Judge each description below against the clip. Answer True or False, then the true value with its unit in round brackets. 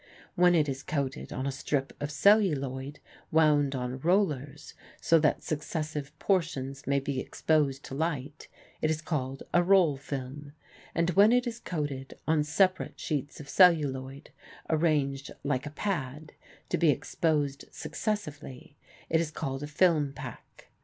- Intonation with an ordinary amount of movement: True (3.1 semitones)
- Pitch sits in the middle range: True (150 Hz)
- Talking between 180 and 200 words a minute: False (145 wpm)